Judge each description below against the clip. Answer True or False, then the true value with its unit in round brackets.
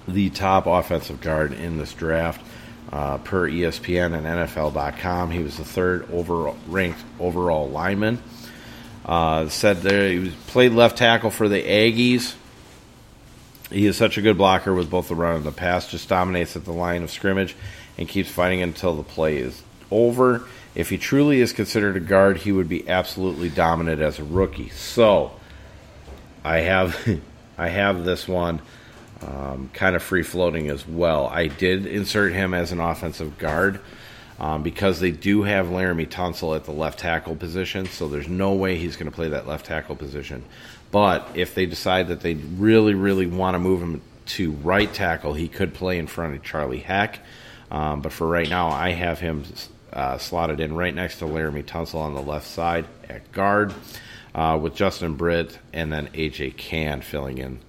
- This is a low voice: True (90 Hz)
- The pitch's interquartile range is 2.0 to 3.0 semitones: False (3.4 semitones)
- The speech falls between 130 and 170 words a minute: False (180 wpm)